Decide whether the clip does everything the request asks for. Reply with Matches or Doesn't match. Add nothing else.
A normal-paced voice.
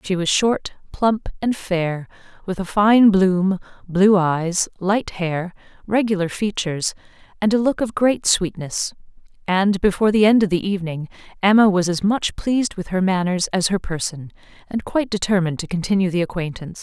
Matches